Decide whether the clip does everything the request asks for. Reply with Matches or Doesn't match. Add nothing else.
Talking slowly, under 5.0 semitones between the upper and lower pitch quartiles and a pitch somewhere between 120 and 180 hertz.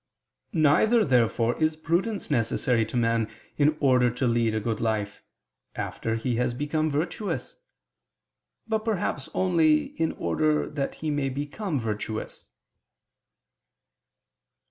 Doesn't match